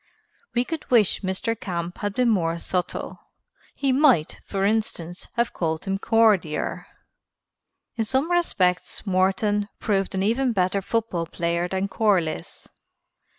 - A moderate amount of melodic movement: Yes, average, 4.1 semitones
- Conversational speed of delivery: No, slow, 130 wpm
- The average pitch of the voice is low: No, high, 195 Hz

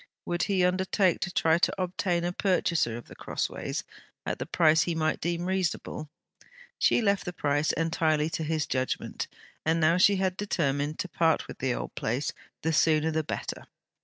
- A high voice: No, medium, 165 Hz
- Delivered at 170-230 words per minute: Yes, average, 180 wpm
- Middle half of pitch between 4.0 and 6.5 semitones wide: No, average, 2.7 semitones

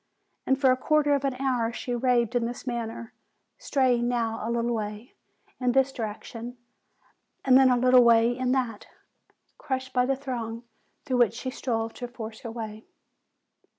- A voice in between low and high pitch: No, high, 245 Hz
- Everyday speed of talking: Yes, average, 170 wpm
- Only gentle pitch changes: Yes, narrow, 2.1 semitones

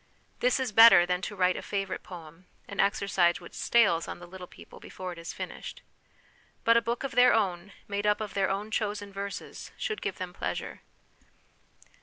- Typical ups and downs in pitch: Yes, average, 3.3 semitones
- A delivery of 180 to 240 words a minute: Yes, average, 190 wpm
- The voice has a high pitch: Yes, high, 200 Hz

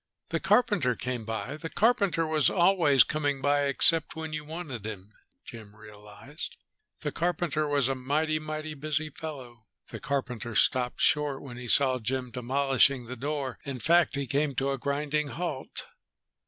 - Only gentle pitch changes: No, average, 3.5 semitones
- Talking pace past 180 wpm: No, average, 160 wpm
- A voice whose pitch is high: No, medium, 140 Hz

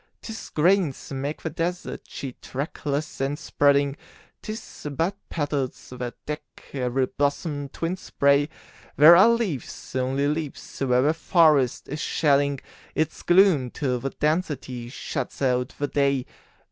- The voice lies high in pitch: No, medium, 145 Hz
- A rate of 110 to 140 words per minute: Yes, slow, 135 wpm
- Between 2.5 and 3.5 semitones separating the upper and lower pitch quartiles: Yes, average, 3.2 semitones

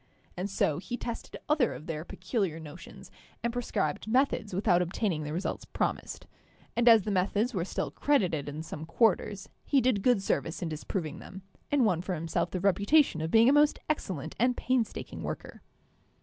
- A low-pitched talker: No, high, 195 Hz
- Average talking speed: Yes, average, 180 wpm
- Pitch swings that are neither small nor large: No, wide, 6.3 semitones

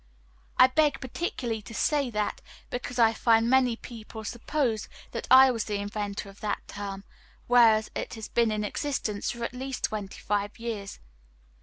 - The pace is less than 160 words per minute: No, average, 165 wpm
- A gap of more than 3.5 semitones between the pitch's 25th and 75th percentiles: No, average, 3.0 semitones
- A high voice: Yes, high, 225 Hz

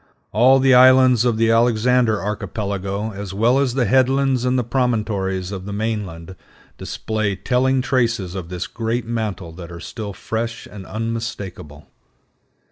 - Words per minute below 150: Yes, average, 140 wpm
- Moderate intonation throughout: Yes, average, 4.1 semitones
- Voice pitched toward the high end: No, low, 110 Hz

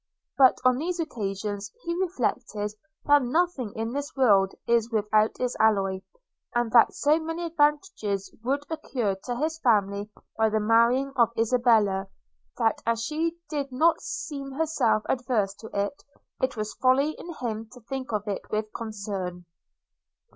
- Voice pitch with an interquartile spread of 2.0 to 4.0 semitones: No, average, 5.1 semitones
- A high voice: Yes, high, 235 Hz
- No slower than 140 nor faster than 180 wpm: Yes, average, 150 wpm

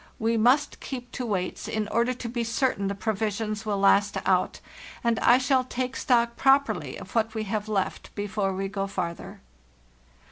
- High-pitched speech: Yes, high, 220 Hz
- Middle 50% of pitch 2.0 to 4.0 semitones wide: Yes, average, 3.4 semitones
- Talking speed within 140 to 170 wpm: No, average, 180 wpm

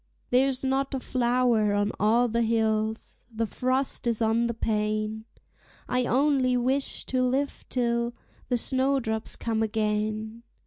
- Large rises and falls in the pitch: No, narrow, 2.6 semitones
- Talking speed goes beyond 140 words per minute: No, slow, 135 wpm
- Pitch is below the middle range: No, high, 235 Hz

